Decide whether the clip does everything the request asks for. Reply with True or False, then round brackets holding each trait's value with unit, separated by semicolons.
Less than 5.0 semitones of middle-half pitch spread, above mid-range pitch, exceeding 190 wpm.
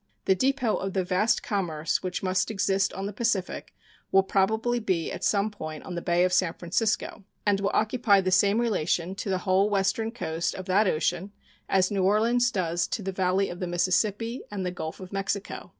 True (2.4 semitones; 195 Hz; 200 wpm)